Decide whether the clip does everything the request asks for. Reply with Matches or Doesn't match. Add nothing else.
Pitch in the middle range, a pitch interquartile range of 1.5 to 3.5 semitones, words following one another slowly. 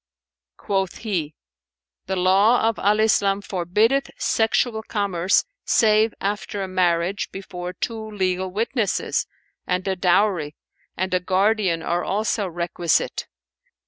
Doesn't match